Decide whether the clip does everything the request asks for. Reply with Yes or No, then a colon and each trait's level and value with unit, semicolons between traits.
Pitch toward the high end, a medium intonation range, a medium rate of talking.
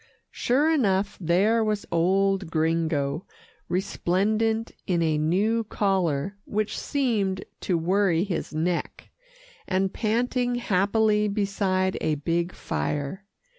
No: high, 195 Hz; average, 4.0 semitones; slow, 105 wpm